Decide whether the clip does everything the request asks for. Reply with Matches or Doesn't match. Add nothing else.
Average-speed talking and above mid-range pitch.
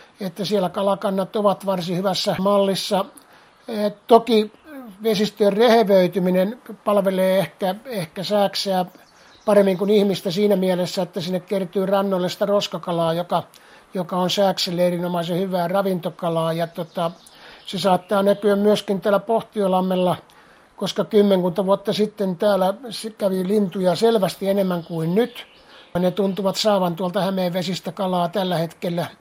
Matches